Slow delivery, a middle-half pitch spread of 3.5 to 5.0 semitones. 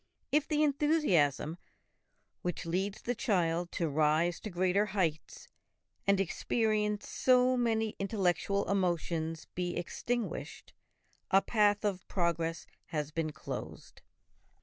Yes: slow, 110 wpm; average, 4.7 semitones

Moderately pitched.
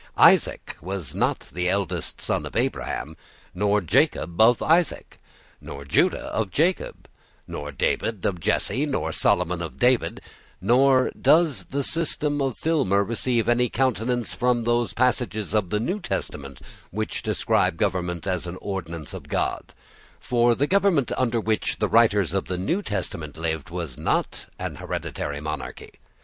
No: low, 105 Hz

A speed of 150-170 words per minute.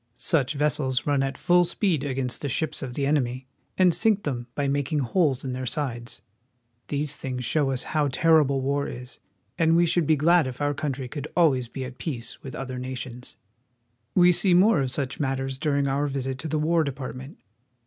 No: average, 195 wpm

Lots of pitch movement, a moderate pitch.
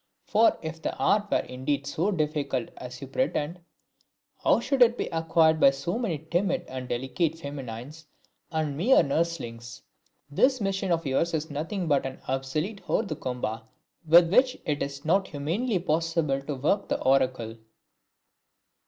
No: average, 4.4 semitones; medium, 155 Hz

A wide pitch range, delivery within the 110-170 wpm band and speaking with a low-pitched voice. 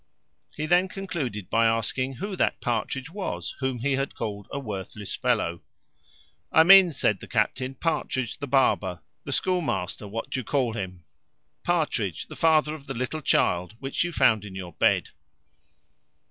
Yes: wide, 6.8 semitones; average, 160 wpm; low, 130 Hz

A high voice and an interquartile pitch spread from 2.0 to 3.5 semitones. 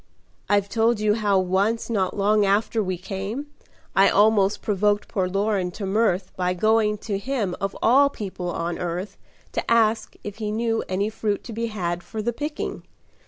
Yes: high, 205 Hz; narrow, 2.5 semitones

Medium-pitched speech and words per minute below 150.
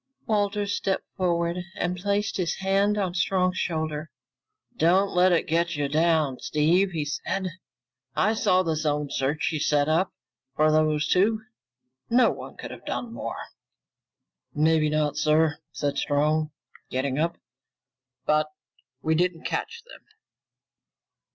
Yes: medium, 165 Hz; slow, 135 wpm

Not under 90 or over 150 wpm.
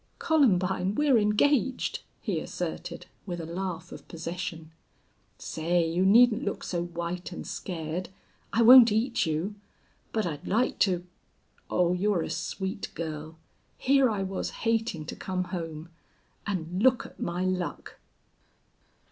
Yes: slow, 135 wpm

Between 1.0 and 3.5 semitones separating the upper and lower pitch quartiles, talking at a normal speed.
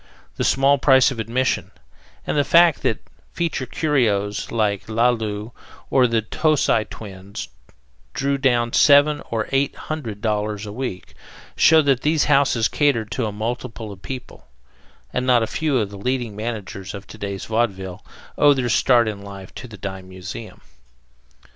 No: average, 4.5 semitones; average, 160 wpm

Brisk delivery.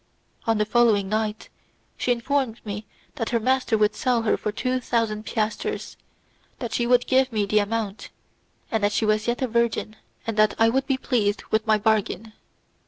No: average, 180 wpm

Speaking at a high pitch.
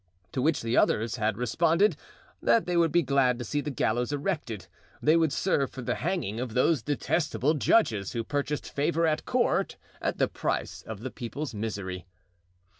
No: medium, 140 Hz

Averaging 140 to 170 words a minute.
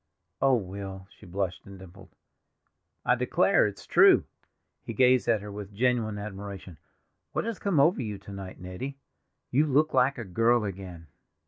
Yes: average, 160 wpm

